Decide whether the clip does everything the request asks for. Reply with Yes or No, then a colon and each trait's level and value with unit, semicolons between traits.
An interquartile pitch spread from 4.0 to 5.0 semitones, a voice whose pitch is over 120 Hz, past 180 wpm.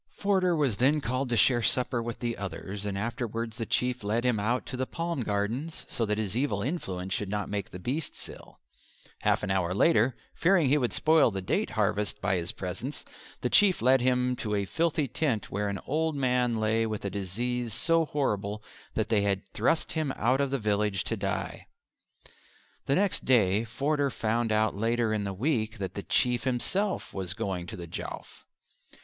No: average, 4.5 semitones; low, 115 Hz; average, 195 wpm